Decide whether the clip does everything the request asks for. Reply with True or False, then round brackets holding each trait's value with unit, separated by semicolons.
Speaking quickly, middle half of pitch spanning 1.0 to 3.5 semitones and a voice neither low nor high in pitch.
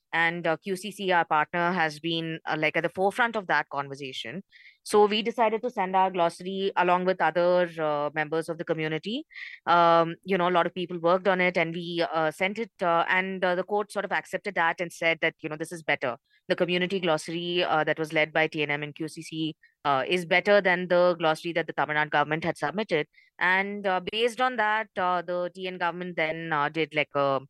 True (220 wpm; 2.9 semitones; 170 Hz)